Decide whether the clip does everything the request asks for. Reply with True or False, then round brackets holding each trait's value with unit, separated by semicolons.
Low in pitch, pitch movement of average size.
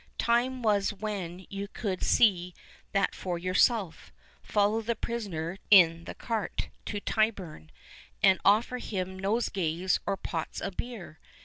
False (200 Hz; 3.4 semitones)